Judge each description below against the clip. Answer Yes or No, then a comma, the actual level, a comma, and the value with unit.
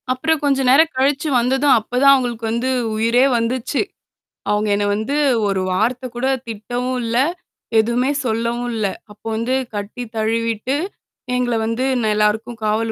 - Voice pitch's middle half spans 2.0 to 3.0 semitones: Yes, average, 2.7 semitones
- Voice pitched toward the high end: Yes, high, 235 Hz